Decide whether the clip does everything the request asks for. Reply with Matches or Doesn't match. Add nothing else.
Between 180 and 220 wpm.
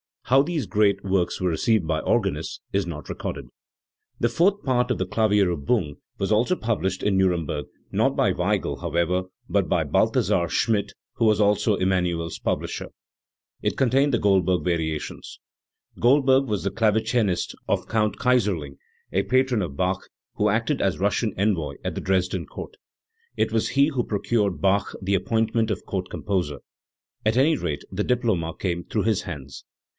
Doesn't match